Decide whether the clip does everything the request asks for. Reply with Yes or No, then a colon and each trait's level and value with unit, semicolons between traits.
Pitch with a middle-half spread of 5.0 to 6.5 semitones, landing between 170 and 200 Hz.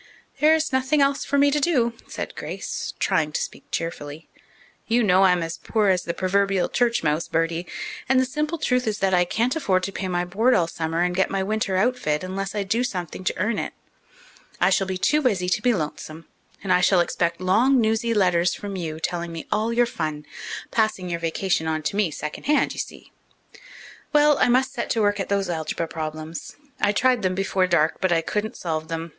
Yes: wide, 5.4 semitones; high, 190 Hz